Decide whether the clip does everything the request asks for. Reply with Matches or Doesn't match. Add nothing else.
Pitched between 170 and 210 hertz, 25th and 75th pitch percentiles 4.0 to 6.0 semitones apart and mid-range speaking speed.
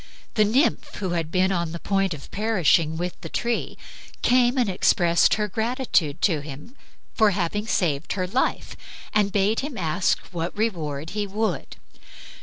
Matches